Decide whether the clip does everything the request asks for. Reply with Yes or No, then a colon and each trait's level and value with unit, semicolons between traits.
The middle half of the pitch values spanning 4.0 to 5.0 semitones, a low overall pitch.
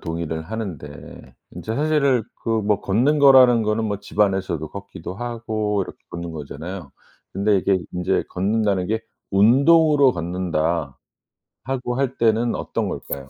No: wide, 5.5 semitones; low, 105 Hz